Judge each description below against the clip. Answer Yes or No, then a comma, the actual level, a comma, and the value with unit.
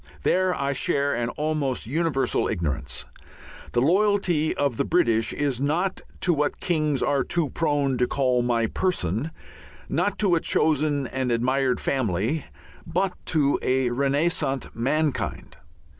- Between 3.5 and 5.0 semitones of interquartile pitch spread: Yes, average, 4.2 semitones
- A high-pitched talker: No, medium, 140 Hz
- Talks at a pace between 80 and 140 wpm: Yes, slow, 135 wpm